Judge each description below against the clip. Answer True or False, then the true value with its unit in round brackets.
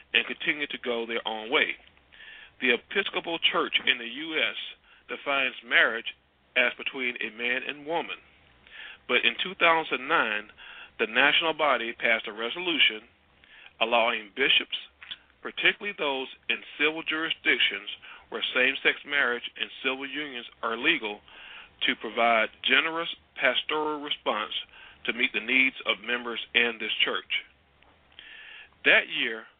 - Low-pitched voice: True (130 Hz)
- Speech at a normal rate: False (125 wpm)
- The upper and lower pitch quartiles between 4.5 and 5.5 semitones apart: True (4.8 semitones)